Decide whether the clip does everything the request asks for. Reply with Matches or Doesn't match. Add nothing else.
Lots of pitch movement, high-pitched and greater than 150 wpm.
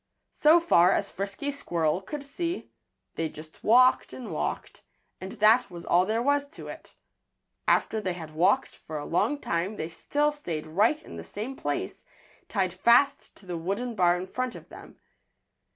Matches